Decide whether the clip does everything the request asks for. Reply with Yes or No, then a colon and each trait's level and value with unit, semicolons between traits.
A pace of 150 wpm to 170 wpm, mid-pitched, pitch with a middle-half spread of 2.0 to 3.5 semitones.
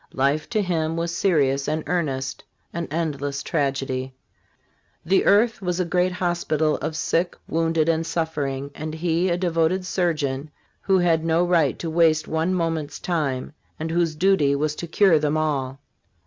Yes: average, 165 wpm; medium, 160 Hz; average, 2.9 semitones